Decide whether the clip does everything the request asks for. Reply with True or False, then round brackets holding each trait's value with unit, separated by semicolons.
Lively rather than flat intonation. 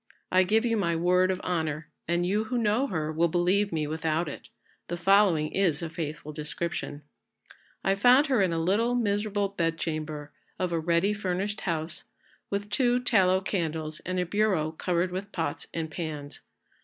False (4.0 semitones)